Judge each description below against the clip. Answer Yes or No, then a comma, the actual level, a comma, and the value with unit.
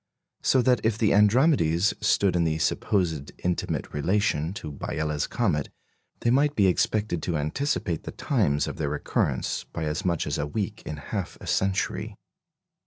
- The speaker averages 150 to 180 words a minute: Yes, average, 165 wpm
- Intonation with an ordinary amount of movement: No, wide, 5.8 semitones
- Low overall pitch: Yes, very low, 90 Hz